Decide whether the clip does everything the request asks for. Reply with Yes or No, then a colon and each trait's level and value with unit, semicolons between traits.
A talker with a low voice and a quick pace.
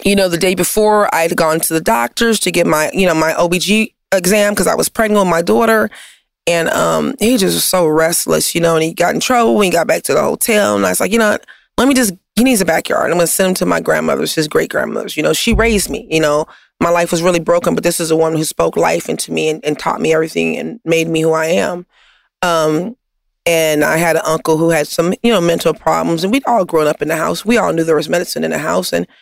No: medium, 170 Hz; fast, 275 wpm